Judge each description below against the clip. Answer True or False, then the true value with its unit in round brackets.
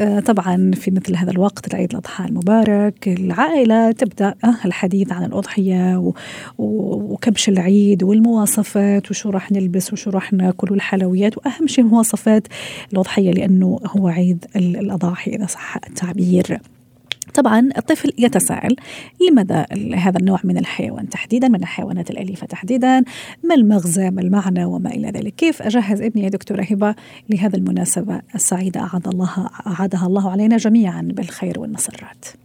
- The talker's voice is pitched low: False (200 Hz)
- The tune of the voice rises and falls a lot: False (2.9 semitones)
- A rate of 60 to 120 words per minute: False (130 wpm)